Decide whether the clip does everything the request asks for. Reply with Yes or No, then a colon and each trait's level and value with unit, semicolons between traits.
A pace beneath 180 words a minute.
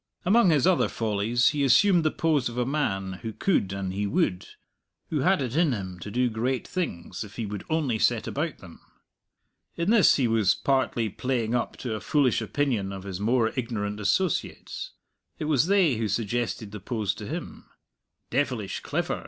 No: average, 185 wpm